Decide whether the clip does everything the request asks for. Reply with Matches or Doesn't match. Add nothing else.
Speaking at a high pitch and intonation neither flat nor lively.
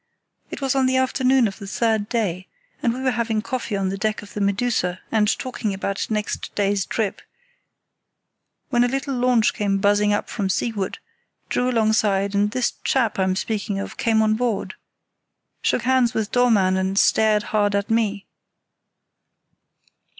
Matches